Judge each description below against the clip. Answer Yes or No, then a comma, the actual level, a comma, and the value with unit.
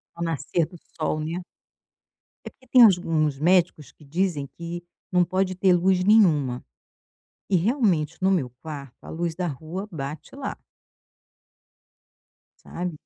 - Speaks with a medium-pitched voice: Yes, medium, 170 Hz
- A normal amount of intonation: Yes, average, 3.4 semitones